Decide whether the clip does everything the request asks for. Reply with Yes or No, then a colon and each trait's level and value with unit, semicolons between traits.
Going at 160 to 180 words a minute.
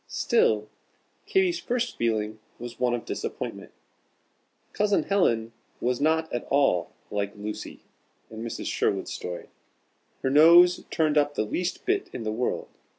No: average, 140 wpm